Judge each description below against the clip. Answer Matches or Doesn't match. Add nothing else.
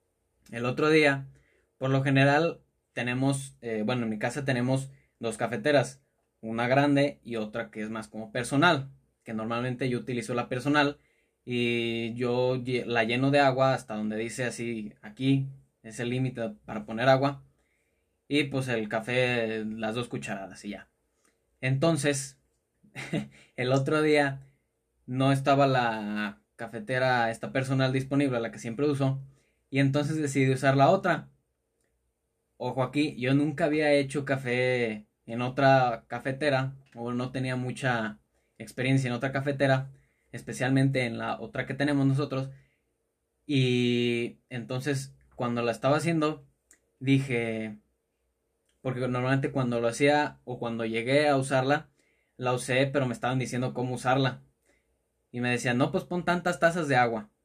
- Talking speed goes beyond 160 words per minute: Doesn't match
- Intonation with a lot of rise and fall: Doesn't match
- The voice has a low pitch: Matches